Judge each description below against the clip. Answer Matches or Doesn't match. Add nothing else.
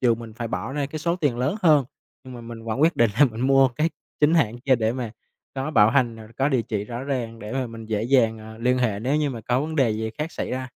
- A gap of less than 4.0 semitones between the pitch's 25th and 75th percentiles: Matches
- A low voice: Matches